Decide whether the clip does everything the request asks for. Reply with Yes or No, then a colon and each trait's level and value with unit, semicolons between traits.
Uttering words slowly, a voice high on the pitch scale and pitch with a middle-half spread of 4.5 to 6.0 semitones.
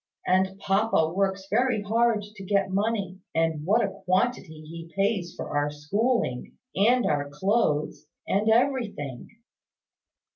Yes: slow, 125 wpm; high, 195 Hz; average, 5.2 semitones